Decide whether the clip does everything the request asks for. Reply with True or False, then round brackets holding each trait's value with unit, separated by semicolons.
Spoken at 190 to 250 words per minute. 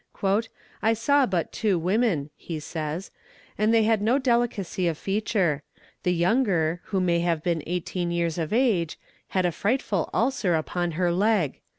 False (160 wpm)